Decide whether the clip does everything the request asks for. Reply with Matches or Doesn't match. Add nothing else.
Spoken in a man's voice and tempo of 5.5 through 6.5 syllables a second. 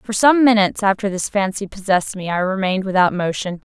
Doesn't match